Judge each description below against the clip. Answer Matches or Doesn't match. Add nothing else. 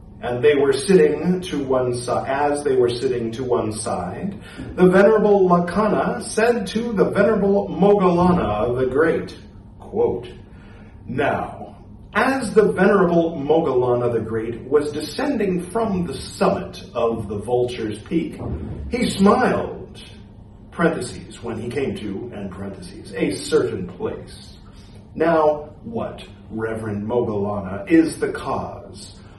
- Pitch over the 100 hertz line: Matches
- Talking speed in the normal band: Doesn't match